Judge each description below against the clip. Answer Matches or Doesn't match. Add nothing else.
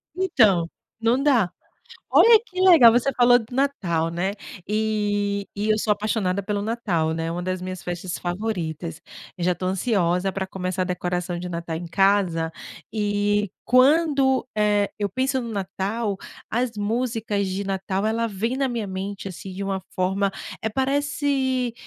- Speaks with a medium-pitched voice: Doesn't match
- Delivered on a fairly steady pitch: Doesn't match